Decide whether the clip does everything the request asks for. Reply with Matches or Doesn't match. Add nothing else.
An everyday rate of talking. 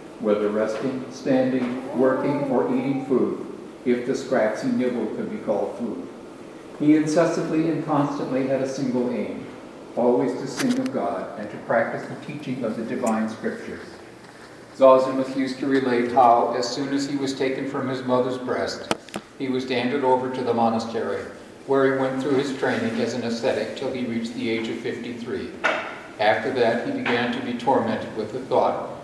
Matches